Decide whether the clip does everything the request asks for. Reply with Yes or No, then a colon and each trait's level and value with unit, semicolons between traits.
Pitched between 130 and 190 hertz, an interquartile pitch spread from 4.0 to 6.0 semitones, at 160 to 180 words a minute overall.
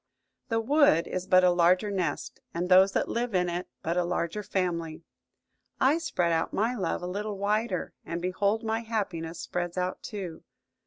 No: medium, 185 Hz; average, 3.5 semitones; average, 175 wpm